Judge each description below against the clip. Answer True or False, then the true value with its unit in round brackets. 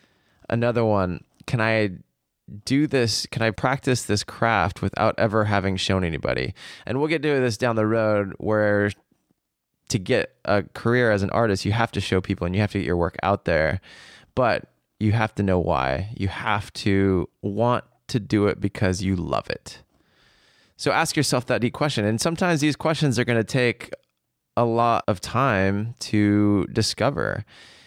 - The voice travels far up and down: False (3.6 semitones)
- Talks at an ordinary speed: True (180 wpm)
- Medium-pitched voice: False (110 Hz)